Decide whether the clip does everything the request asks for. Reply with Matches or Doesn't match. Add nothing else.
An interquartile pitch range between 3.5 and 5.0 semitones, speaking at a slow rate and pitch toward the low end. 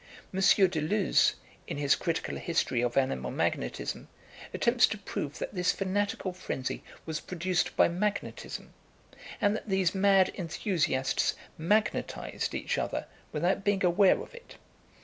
Doesn't match